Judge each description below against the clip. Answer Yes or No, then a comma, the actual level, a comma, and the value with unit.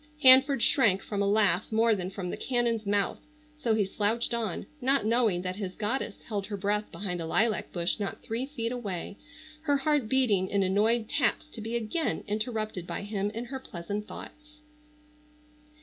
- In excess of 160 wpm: Yes, average, 180 wpm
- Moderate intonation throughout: Yes, average, 3.4 semitones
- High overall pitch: Yes, high, 215 Hz